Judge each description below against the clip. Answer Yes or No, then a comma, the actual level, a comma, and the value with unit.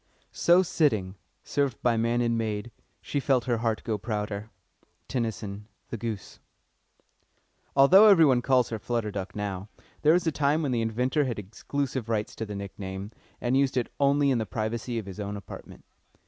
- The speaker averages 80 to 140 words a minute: No, average, 175 wpm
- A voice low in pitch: Yes, low, 115 Hz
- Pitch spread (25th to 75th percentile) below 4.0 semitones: No, average, 4.5 semitones